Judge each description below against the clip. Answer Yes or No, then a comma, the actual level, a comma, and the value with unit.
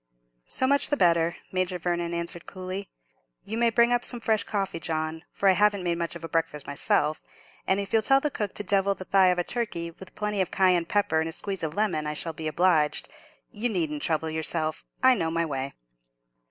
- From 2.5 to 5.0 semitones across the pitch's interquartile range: Yes, average, 4.0 semitones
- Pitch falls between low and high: Yes, medium, 180 Hz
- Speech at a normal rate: No, fast, 220 wpm